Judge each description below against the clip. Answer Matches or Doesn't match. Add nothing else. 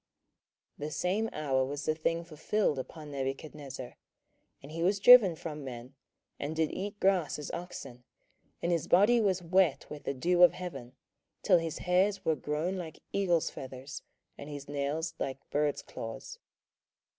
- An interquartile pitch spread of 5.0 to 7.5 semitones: Doesn't match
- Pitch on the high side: Doesn't match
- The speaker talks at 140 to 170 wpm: Matches